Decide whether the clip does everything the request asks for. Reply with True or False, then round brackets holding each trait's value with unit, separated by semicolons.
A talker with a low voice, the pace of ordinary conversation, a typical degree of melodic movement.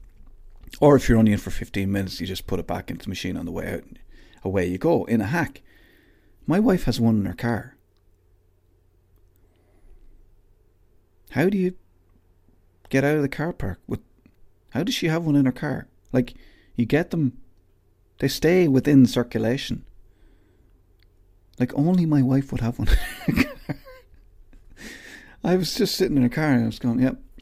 False (110 Hz; 180 wpm; 6.9 semitones)